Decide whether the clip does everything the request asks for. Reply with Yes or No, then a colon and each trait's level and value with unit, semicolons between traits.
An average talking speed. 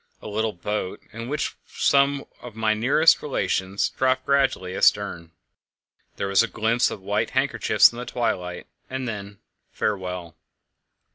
Yes: average, 145 wpm